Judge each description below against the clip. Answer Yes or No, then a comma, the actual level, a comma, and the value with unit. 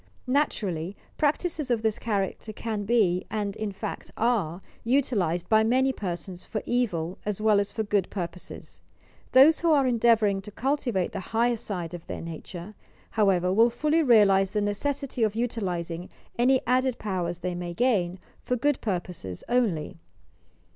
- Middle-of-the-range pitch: No, high, 210 Hz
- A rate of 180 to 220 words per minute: No, average, 155 wpm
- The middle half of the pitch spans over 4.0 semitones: Yes, average, 5.0 semitones